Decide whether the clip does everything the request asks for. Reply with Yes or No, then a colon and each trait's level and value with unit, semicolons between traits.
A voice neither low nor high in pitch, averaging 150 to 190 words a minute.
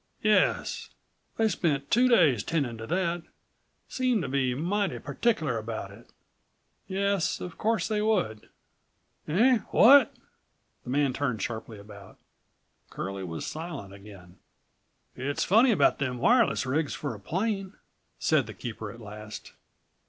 No: medium, 145 Hz; slow, 135 wpm